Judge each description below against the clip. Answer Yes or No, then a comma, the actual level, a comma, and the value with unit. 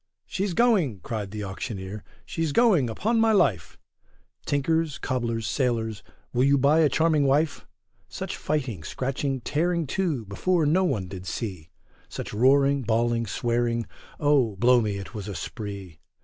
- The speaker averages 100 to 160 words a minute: Yes, average, 150 wpm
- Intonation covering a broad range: Yes, wide, 6.0 semitones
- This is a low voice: Yes, low, 125 Hz